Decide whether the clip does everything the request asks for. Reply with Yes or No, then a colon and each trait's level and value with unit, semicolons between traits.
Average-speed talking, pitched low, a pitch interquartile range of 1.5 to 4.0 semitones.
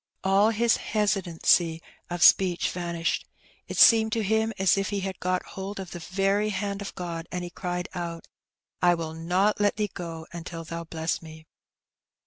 No: average, 175 wpm; medium, 180 Hz; average, 3.1 semitones